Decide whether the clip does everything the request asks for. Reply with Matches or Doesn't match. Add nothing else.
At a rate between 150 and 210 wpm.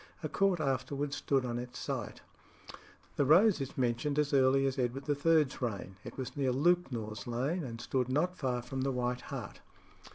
Matches